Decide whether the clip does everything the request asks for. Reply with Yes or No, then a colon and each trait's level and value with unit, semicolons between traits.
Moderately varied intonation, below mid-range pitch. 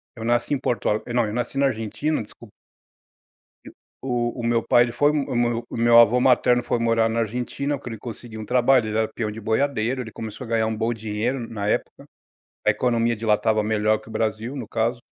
No: narrow, 1.8 semitones; low, 115 Hz